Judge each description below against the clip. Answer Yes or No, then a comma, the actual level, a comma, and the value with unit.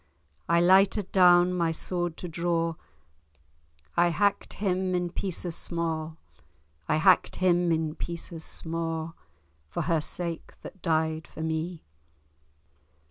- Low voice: No, medium, 170 Hz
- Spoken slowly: Yes, slow, 120 wpm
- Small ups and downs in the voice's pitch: Yes, narrow, 1.8 semitones